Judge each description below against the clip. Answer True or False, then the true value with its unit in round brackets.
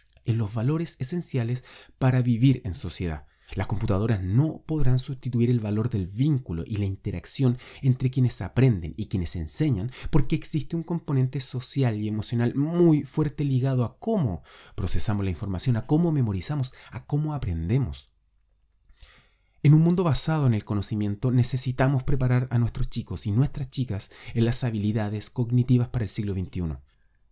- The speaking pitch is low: True (120 Hz)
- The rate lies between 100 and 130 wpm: False (155 wpm)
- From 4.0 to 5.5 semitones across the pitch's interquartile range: True (5.1 semitones)